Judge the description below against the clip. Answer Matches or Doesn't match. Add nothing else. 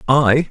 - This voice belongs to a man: Matches